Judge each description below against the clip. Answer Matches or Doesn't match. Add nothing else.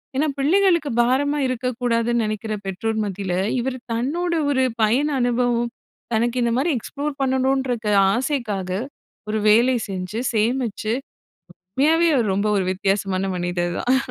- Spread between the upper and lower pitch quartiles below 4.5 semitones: Matches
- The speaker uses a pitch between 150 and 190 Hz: Doesn't match